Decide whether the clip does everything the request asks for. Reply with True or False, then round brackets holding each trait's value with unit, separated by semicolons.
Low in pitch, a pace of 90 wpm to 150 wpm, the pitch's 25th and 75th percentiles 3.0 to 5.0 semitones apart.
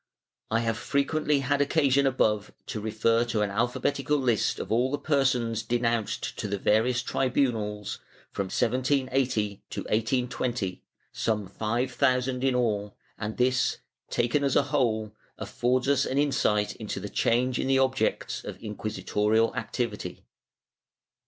True (120 Hz; 140 wpm; 3.5 semitones)